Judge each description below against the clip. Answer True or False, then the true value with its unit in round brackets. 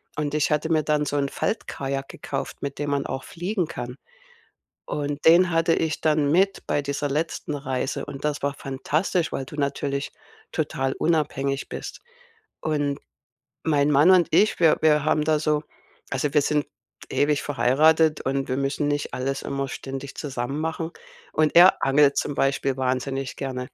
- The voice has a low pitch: False (145 Hz)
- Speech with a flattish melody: True (2.2 semitones)